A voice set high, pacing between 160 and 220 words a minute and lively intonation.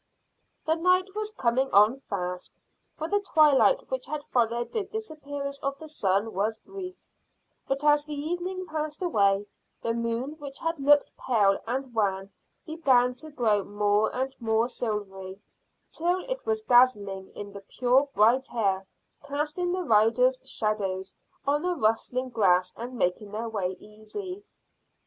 No: very high, 255 Hz; average, 150 wpm; wide, 6.7 semitones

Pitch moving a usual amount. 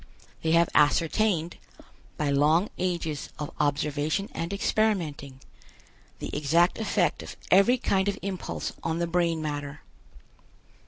Yes: average, 4.2 semitones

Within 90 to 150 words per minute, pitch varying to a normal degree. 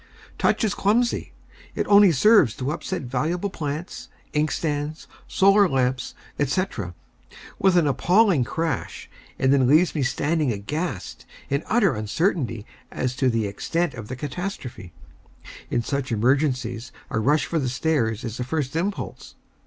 No: average, 140 wpm; wide, 5.7 semitones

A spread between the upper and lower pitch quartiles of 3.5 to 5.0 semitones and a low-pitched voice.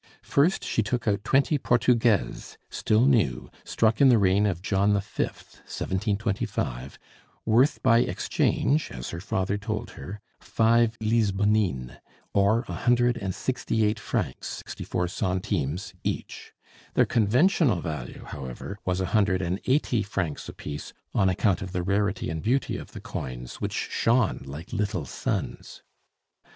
Yes: average, 4.2 semitones; low, 105 Hz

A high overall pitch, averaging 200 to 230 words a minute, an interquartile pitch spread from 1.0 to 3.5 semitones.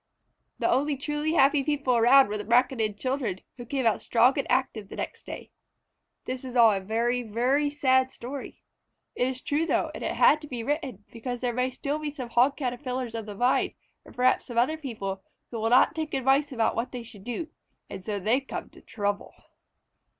Yes: very high, 250 Hz; fast, 205 wpm; average, 3.2 semitones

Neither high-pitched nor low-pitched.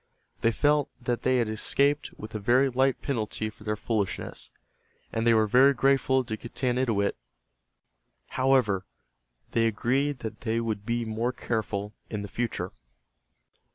No: low, 115 Hz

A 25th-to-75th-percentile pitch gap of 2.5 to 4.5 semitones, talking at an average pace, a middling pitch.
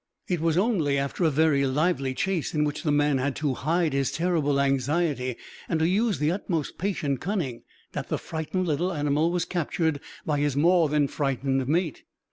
Yes: average, 3.7 semitones; average, 185 wpm; medium, 150 Hz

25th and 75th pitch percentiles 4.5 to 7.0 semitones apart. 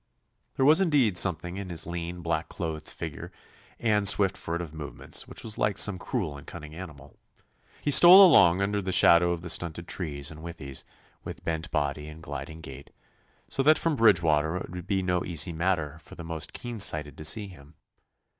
No: average, 4.1 semitones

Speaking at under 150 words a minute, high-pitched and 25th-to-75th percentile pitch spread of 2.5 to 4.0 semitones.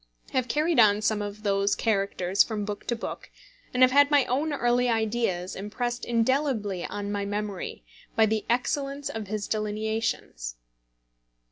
No: average, 155 wpm; high, 220 Hz; average, 3.3 semitones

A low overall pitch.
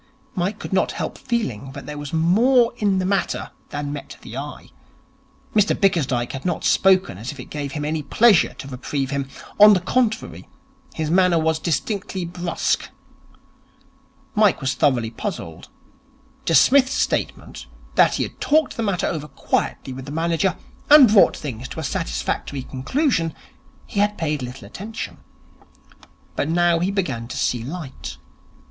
No: medium, 165 Hz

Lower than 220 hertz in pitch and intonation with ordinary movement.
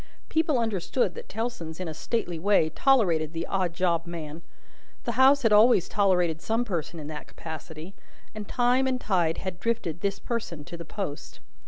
No: medium, 185 Hz; wide, 5.9 semitones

